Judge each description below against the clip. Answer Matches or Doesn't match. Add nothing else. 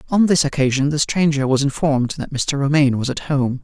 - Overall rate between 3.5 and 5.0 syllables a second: Doesn't match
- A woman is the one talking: Doesn't match